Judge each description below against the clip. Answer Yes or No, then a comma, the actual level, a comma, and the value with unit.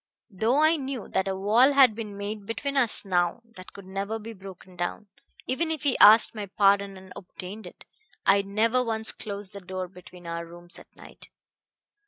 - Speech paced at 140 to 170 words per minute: No, average, 190 wpm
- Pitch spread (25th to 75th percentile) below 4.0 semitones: Yes, average, 3.3 semitones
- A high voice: Yes, high, 200 Hz